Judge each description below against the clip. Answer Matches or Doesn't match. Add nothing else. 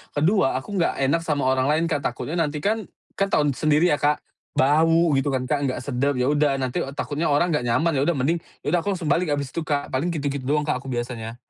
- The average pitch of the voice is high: Doesn't match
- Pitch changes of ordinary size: Matches